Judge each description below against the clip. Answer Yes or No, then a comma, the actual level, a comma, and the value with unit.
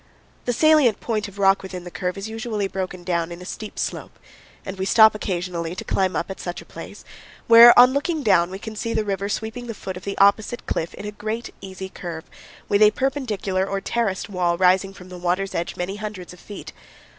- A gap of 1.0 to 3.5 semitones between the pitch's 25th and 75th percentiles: Yes, average, 3.1 semitones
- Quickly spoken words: Yes, fast, 220 wpm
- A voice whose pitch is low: No, high, 195 Hz